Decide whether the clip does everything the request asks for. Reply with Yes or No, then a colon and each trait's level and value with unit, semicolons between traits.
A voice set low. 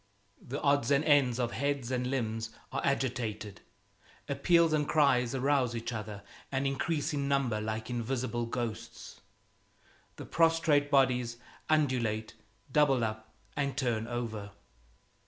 Yes: low, 125 Hz